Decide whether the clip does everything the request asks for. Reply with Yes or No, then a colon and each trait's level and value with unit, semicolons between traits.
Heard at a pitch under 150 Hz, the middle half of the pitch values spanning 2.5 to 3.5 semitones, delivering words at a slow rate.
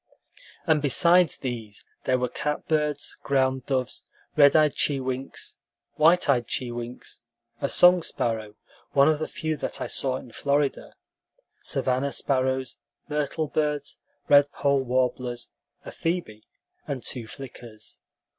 Yes: low, 135 Hz; average, 2.9 semitones; slow, 120 wpm